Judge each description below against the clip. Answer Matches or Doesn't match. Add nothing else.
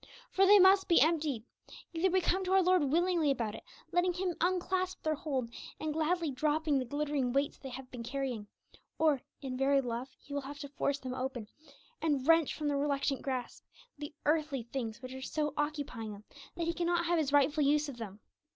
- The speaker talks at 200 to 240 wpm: Matches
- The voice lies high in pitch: Matches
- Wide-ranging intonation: Doesn't match